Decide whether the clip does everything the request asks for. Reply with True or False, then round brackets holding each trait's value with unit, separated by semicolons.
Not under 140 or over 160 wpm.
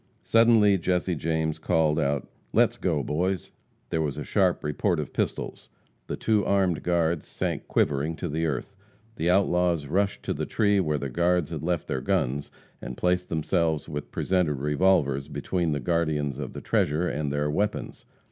False (170 wpm)